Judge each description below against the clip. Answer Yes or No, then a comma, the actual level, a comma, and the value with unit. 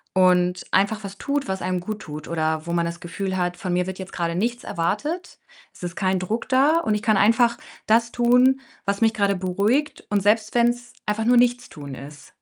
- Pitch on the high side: Yes, high, 200 Hz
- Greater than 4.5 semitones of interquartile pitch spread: Yes, average, 4.9 semitones